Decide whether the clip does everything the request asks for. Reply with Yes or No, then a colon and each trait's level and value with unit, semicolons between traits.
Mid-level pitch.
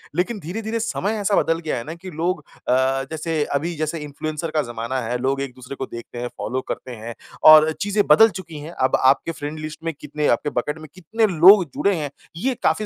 Yes: medium, 155 Hz